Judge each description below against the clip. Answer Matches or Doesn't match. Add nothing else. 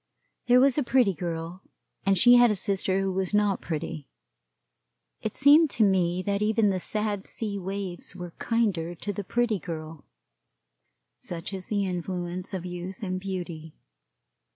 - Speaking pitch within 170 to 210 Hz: Matches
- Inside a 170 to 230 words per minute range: Doesn't match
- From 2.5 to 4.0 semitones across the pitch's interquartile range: Matches